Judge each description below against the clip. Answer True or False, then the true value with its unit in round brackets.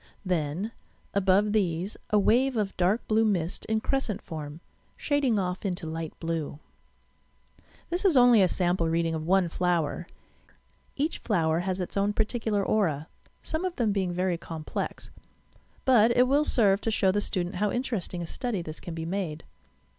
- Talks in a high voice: True (195 Hz)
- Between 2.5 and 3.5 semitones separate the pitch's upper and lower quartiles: False (4.6 semitones)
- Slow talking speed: False (165 wpm)